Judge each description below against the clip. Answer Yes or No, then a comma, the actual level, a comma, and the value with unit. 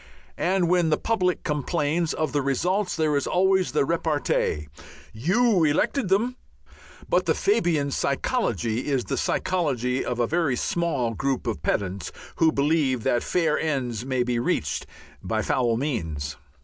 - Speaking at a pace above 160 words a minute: No, average, 150 wpm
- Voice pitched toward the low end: No, medium, 145 Hz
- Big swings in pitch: Yes, wide, 6.0 semitones